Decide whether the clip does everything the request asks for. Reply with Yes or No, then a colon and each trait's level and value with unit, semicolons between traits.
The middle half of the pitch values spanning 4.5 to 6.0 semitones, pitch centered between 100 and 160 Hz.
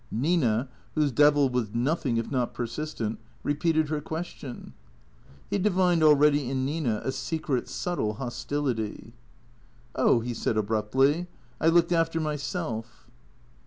Yes: average, 4.9 semitones; medium, 140 Hz